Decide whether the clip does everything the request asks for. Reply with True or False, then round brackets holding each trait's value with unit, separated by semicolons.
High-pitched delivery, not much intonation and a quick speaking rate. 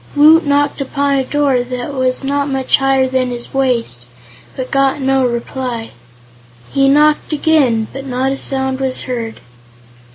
False (265 Hz; 1.8 semitones; 155 wpm)